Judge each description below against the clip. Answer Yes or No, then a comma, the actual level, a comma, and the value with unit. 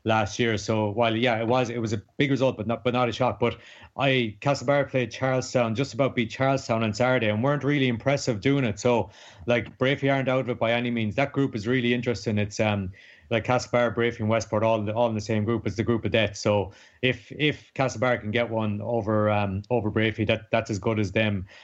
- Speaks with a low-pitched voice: Yes, low, 115 Hz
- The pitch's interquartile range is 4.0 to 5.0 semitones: No, narrow, 2.6 semitones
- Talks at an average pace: No, fast, 235 wpm